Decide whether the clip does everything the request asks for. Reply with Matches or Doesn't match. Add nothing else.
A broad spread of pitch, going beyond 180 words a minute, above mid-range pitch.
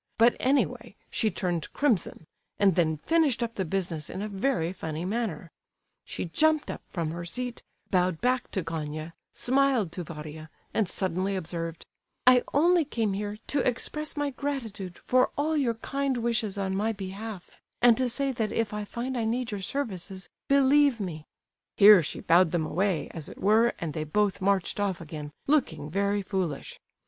Doesn't match